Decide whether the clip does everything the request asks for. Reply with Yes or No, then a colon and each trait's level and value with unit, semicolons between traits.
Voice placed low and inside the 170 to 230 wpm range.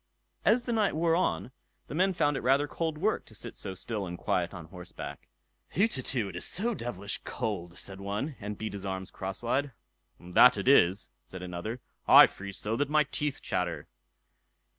Yes: low, 110 Hz; average, 185 wpm